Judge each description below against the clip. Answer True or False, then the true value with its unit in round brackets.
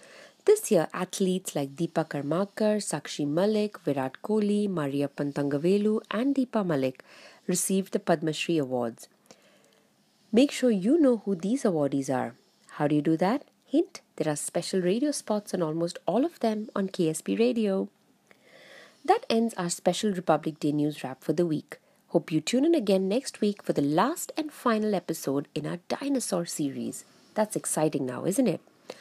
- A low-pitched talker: False (185 Hz)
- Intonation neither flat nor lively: False (6.2 semitones)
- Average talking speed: True (165 wpm)